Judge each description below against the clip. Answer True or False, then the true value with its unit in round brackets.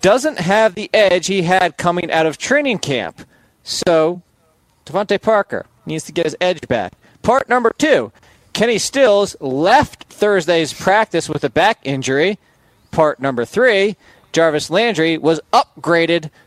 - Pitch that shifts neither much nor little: True (4.2 semitones)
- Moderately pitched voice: True (170 Hz)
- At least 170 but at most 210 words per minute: False (140 wpm)